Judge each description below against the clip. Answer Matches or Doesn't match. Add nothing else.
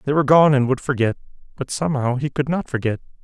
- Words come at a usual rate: Doesn't match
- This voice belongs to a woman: Doesn't match